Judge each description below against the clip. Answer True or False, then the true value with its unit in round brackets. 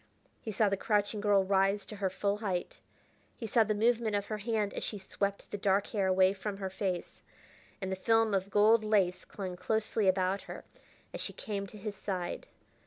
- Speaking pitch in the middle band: False (200 Hz)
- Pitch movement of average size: False (2.0 semitones)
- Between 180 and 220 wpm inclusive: True (200 wpm)